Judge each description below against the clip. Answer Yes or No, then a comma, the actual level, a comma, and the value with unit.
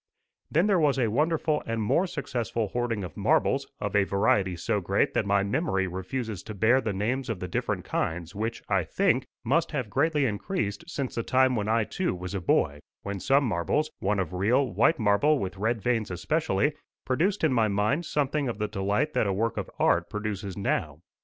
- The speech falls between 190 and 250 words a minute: Yes, average, 200 wpm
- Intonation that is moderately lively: No, wide, 5.8 semitones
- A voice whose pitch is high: No, low, 110 Hz